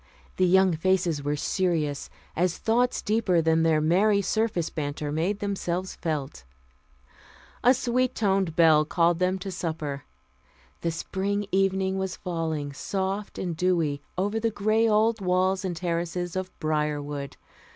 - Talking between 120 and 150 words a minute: Yes, average, 140 wpm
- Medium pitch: Yes, medium, 180 Hz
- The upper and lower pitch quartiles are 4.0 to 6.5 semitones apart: No, average, 3.5 semitones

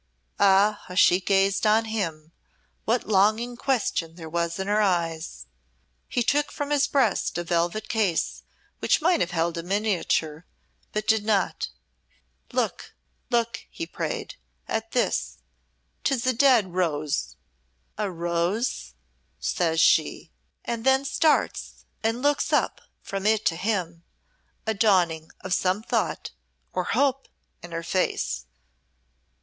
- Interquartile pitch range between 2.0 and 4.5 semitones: No, average, 5.0 semitones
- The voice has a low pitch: No, high, 200 Hz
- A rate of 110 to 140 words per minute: Yes, slow, 135 wpm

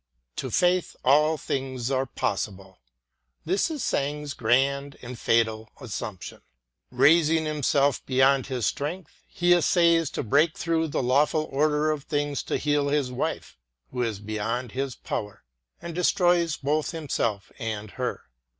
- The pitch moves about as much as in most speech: Yes, average, 4.0 semitones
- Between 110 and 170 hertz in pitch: Yes, medium, 140 Hz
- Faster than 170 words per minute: No, average, 150 wpm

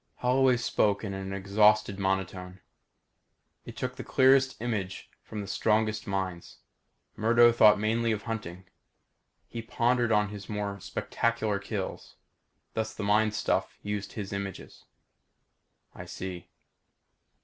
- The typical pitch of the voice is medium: No, low, 105 Hz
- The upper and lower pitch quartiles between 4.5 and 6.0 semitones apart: No, average, 2.7 semitones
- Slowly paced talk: Yes, slow, 125 wpm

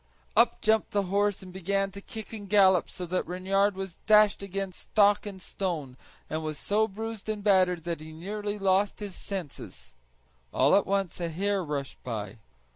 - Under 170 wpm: No, average, 180 wpm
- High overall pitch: Yes, high, 195 Hz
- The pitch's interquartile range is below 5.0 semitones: Yes, average, 2.7 semitones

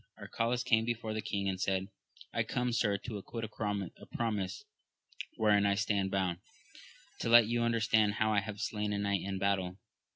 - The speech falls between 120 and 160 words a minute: No, average, 175 wpm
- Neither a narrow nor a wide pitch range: No, narrow, 2.3 semitones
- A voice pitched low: Yes, low, 105 Hz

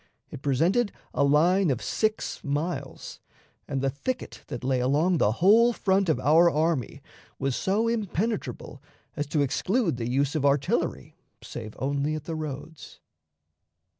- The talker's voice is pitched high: No, medium, 150 Hz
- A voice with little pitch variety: No, wide, 5.5 semitones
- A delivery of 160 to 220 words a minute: No, average, 145 wpm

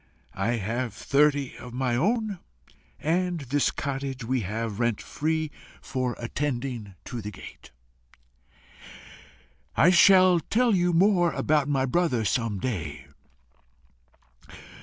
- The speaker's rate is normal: No, slow, 115 wpm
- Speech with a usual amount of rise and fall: No, wide, 6.0 semitones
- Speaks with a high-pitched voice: No, low, 135 Hz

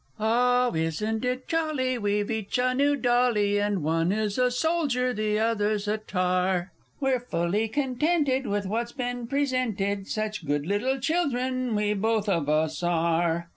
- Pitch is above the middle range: Yes, high, 220 Hz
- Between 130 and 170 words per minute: Yes, average, 150 wpm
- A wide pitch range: No, average, 4.3 semitones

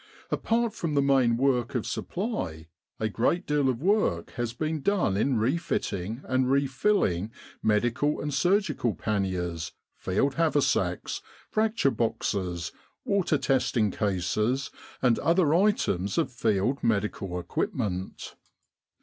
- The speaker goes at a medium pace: No, slow, 115 wpm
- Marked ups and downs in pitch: Yes, wide, 7.1 semitones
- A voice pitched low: Yes, low, 125 Hz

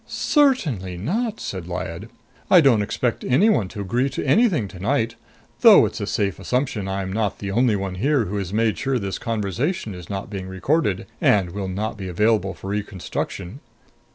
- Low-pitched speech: Yes, low, 105 Hz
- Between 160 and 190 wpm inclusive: Yes, average, 175 wpm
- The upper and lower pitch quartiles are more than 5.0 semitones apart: Yes, wide, 5.4 semitones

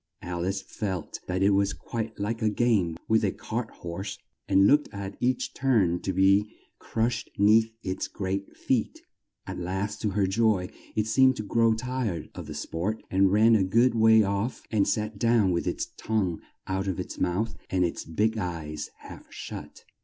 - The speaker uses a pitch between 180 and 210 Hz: No, low, 100 Hz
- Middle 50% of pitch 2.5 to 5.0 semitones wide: Yes, average, 3.0 semitones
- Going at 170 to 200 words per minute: Yes, average, 185 wpm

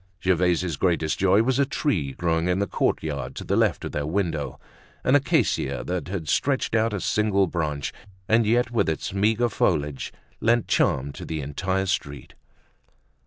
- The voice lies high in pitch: No, very low, 90 Hz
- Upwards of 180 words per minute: No, average, 165 wpm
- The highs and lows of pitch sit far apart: Yes, wide, 6.0 semitones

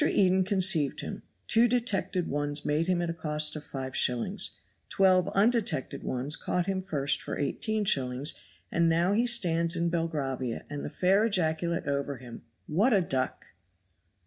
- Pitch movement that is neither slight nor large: Yes, average, 4.8 semitones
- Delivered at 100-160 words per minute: Yes, average, 150 wpm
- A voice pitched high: No, medium, 170 Hz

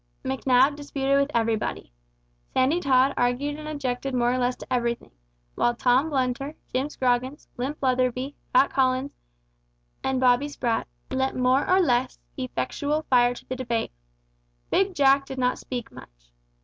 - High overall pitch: Yes, very high, 260 Hz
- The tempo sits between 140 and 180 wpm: Yes, average, 150 wpm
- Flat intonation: Yes, narrow, 2.1 semitones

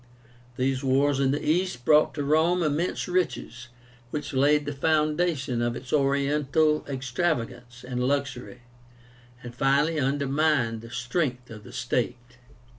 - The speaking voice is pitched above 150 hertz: No, medium, 140 Hz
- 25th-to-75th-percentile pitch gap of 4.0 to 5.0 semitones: No, average, 3.5 semitones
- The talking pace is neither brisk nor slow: No, slow, 130 wpm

